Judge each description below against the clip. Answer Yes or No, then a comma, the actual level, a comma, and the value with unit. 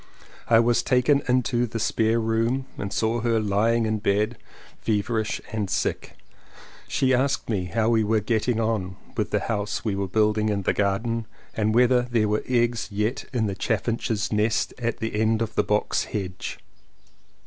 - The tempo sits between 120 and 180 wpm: Yes, average, 175 wpm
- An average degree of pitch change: No, narrow, 1.9 semitones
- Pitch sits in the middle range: No, low, 110 Hz